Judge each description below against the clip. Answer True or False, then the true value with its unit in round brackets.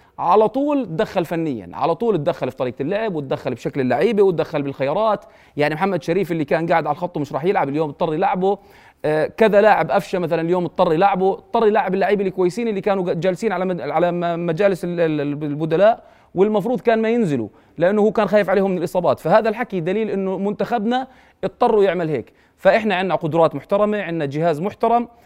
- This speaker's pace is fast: True (175 wpm)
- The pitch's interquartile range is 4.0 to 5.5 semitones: True (4.6 semitones)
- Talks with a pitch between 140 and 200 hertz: True (185 Hz)